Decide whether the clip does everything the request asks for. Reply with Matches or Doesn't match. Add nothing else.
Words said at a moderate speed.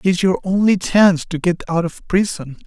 Doesn't match